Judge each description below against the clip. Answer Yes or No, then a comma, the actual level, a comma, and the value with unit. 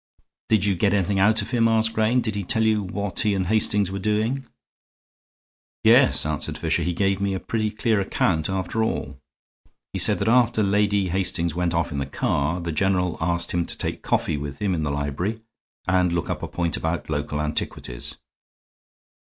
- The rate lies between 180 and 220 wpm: Yes, average, 190 wpm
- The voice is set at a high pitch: No, very low, 95 Hz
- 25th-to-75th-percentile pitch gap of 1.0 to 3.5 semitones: No, average, 3.9 semitones